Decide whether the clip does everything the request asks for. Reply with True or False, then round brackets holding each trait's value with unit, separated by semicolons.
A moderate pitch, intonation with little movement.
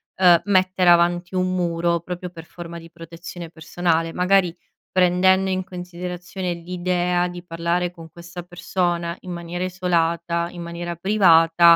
True (175 Hz; 1.1 semitones)